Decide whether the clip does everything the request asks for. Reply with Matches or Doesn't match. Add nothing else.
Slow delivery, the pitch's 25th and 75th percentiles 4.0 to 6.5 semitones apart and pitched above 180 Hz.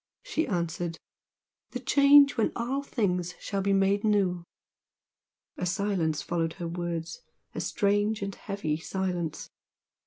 Doesn't match